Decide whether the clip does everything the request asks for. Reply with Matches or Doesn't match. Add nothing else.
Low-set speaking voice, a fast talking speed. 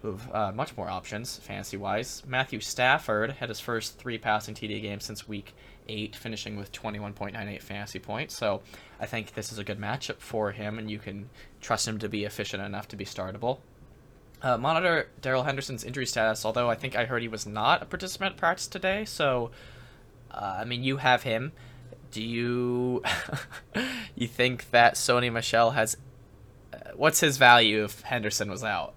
Doesn't match